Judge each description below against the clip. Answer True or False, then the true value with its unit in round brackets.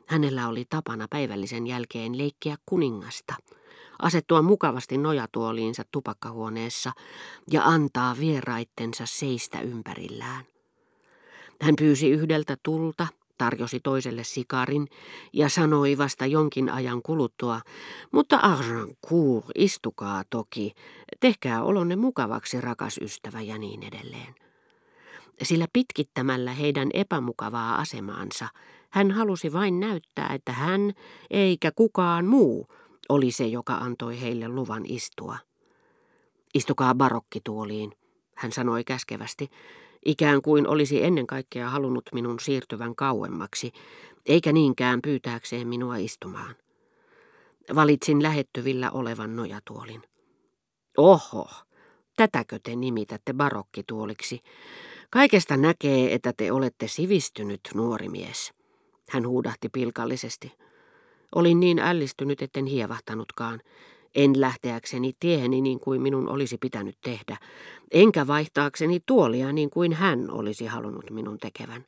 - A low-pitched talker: True (130 Hz)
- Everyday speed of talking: True (105 wpm)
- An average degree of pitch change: True (4.8 semitones)